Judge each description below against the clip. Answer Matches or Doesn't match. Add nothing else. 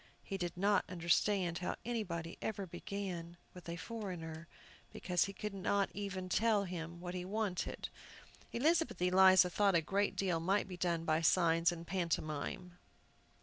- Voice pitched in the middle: Matches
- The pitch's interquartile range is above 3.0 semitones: Doesn't match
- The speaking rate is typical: Matches